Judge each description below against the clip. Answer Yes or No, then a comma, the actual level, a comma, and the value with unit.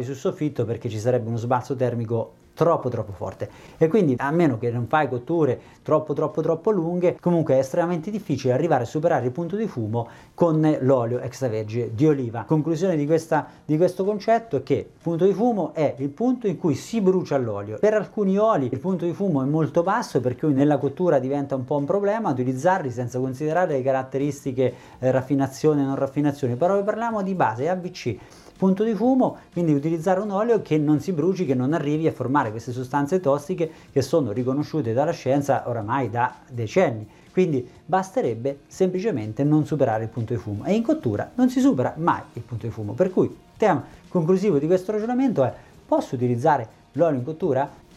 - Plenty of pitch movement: Yes, wide, 5.9 semitones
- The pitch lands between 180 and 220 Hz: No, medium, 150 Hz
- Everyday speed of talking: No, fast, 195 wpm